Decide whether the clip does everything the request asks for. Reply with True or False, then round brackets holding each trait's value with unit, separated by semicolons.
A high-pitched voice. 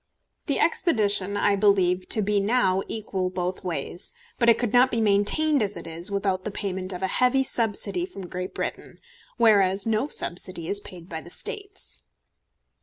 True (200 Hz)